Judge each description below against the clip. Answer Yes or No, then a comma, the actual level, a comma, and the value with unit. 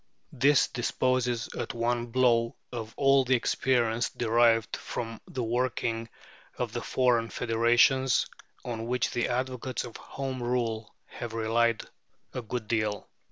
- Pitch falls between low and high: No, low, 120 Hz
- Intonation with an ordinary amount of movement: No, narrow, 1.8 semitones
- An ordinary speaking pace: No, slow, 130 wpm